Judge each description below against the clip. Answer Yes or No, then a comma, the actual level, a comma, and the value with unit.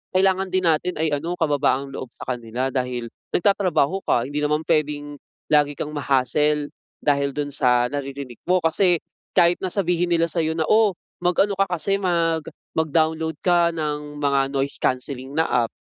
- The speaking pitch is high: No, medium, 150 Hz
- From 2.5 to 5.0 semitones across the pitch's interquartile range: Yes, average, 3.6 semitones